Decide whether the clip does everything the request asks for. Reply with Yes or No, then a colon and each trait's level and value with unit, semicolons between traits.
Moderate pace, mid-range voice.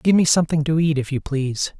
No: fast, 265 wpm; medium, 150 Hz